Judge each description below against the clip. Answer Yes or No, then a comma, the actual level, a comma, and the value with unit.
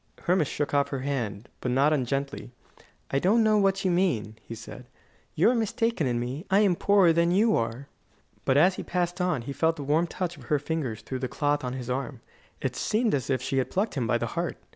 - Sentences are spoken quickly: Yes, fast, 230 wpm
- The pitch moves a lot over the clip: Yes, wide, 5.8 semitones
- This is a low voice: No, medium, 145 Hz